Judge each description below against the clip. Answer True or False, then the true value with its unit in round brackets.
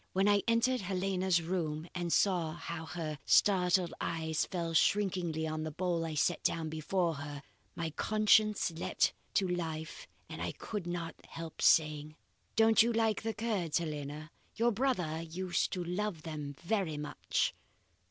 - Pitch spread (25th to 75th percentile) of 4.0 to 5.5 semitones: False (3.6 semitones)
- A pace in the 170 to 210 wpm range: False (150 wpm)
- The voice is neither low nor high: True (170 Hz)